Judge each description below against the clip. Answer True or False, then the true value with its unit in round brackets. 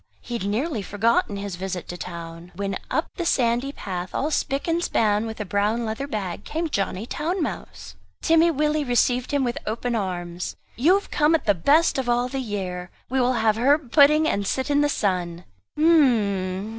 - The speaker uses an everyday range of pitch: False (6.5 semitones)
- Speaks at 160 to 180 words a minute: False (195 wpm)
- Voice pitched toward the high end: True (230 Hz)